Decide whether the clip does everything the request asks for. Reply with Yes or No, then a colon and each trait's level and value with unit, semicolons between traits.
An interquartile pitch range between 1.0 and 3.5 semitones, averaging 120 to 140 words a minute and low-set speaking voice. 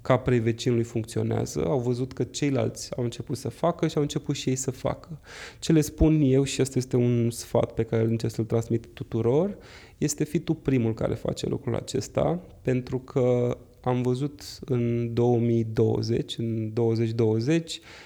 No: average, 3.1 semitones; average, 165 wpm; low, 125 Hz